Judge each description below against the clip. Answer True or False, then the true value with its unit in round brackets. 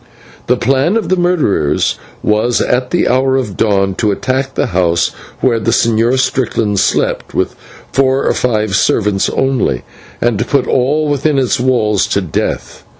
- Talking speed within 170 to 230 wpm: False (160 wpm)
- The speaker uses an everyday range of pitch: True (4.0 semitones)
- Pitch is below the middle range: True (125 Hz)